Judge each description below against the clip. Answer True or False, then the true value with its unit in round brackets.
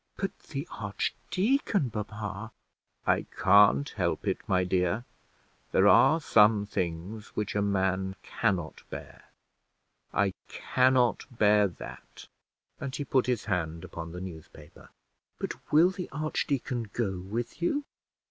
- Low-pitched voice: True (105 Hz)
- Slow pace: True (125 wpm)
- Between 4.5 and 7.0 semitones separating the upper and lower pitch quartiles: True (5.4 semitones)